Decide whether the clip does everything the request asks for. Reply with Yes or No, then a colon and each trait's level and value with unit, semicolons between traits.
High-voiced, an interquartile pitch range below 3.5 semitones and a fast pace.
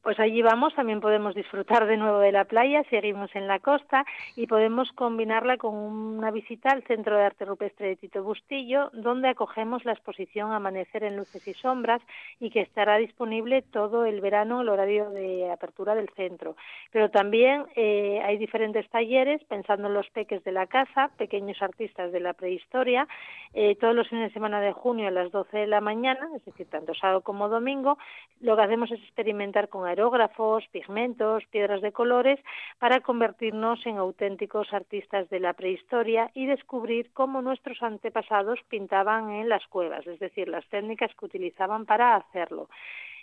No: high, 220 Hz; average, 2.9 semitones; average, 175 wpm